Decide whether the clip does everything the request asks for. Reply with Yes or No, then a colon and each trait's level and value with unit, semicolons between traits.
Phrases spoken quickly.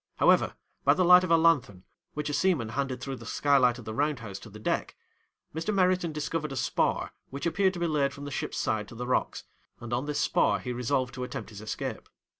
Yes: fast, 230 wpm